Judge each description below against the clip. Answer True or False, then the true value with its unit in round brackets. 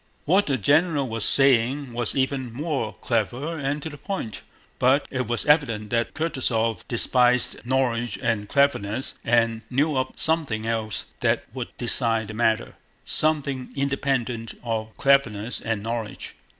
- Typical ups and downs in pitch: True (3.6 semitones)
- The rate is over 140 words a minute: False (135 wpm)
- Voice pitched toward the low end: True (125 Hz)